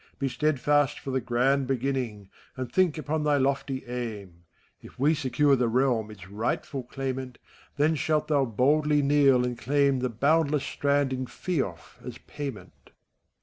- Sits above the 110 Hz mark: Yes, low, 135 Hz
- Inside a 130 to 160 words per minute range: Yes, average, 155 wpm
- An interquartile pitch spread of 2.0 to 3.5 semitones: Yes, average, 3.0 semitones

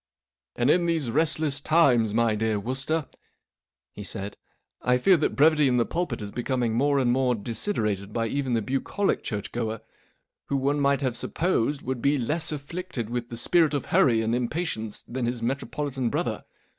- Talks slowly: No, average, 180 wpm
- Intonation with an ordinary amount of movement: Yes, average, 4.3 semitones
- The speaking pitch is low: Yes, low, 130 Hz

